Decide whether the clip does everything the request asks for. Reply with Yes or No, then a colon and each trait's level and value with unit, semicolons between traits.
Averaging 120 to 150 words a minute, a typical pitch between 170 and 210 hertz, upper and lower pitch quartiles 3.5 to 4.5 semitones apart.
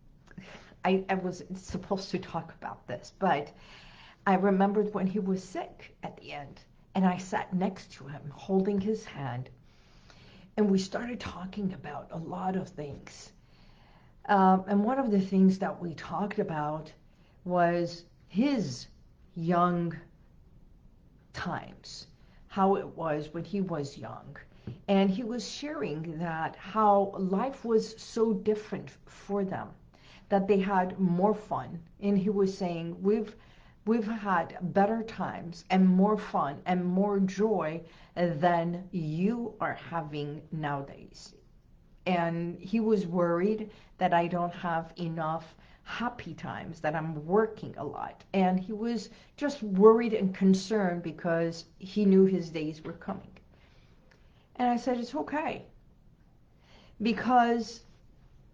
Yes: slow, 135 wpm; high, 190 Hz; average, 3.8 semitones